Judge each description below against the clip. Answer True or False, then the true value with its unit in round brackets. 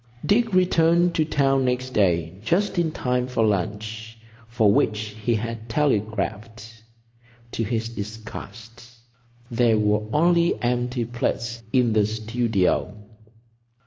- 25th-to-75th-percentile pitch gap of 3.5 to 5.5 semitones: False (2.8 semitones)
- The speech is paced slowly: True (115 wpm)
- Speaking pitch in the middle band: False (115 Hz)